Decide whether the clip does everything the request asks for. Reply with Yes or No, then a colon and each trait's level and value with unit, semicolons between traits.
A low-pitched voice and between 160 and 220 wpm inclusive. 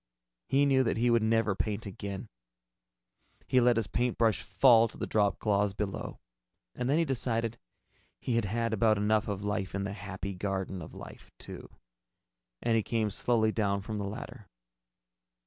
Yes: low, 110 Hz; average, 165 wpm